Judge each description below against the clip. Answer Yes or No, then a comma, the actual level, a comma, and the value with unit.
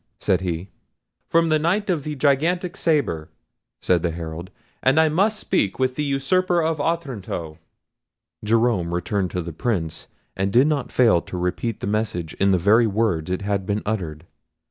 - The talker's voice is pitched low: Yes, low, 110 Hz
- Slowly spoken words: No, average, 170 wpm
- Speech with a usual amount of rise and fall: No, wide, 8.8 semitones